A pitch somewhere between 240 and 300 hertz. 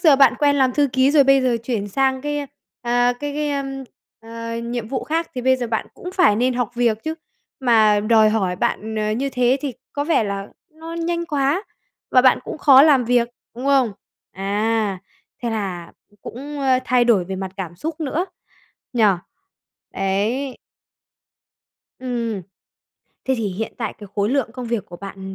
Yes: high, 245 Hz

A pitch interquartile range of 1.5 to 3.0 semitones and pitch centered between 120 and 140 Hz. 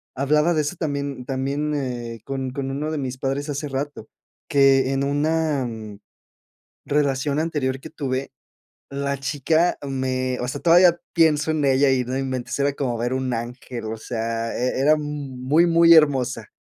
Yes: narrow, 2.5 semitones; low, 135 Hz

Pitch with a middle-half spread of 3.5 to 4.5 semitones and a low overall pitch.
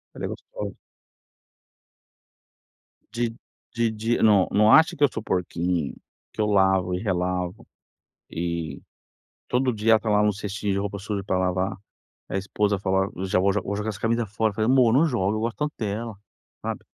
No: average, 3.0 semitones; low, 105 Hz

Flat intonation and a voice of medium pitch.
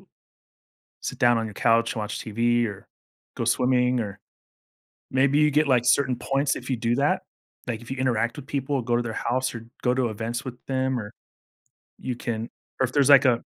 No: narrow, 2.2 semitones; low, 125 Hz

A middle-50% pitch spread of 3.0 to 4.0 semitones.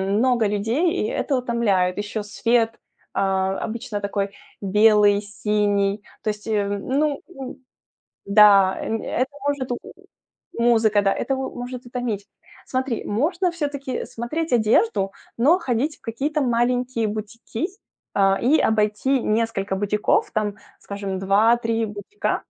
Yes: average, 3.7 semitones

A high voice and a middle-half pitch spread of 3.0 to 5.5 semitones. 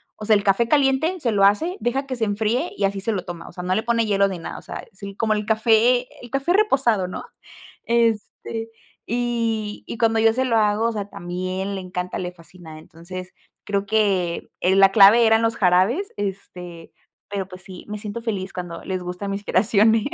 Yes: high, 210 Hz; average, 3.6 semitones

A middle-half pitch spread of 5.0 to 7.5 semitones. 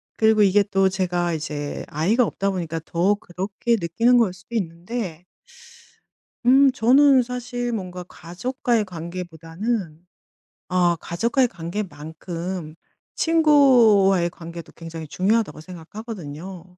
Yes: average, 5.3 semitones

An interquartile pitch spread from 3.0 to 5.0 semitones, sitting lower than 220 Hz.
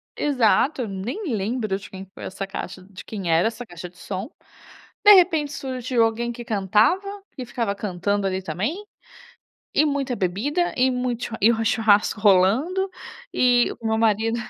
No: average, 4.7 semitones; high, 225 Hz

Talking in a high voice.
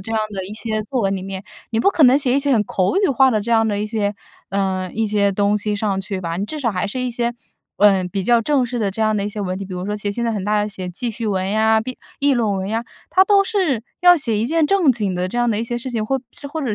Yes: high, 220 Hz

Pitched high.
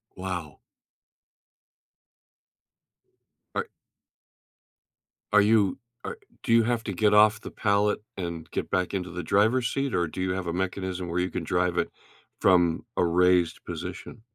No: very low, 95 Hz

